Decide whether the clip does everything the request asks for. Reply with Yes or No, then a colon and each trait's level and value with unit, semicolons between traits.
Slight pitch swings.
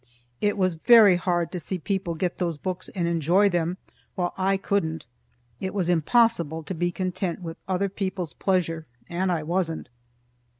Yes: narrow, 2.3 semitones